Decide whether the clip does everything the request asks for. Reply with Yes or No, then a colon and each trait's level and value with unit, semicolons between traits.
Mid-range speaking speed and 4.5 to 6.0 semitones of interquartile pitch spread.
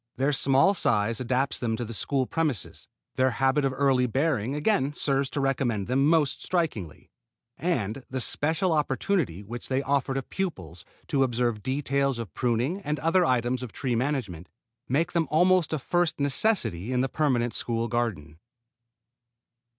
No: average, 160 wpm; average, 3.9 semitones